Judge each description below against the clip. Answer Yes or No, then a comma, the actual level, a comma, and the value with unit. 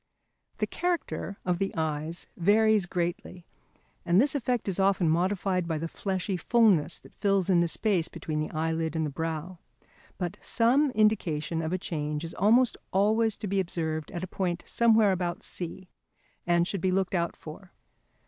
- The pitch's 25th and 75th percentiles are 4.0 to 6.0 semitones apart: No, average, 3.6 semitones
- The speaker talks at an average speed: Yes, average, 165 wpm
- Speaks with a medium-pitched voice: Yes, medium, 180 Hz